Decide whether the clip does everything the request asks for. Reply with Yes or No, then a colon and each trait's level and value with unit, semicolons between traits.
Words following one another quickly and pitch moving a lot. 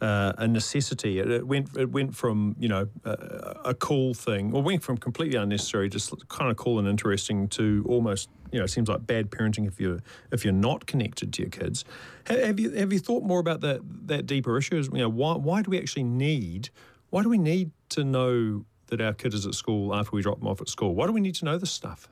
Yes: fast, 245 wpm; wide, 6.3 semitones